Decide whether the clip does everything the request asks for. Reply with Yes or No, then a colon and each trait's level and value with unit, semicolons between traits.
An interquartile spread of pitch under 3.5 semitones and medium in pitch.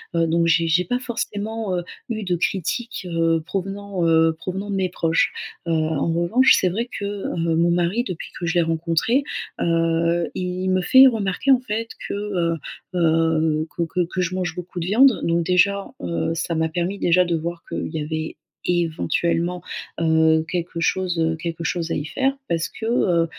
Yes: average, 3.0 semitones; medium, 175 Hz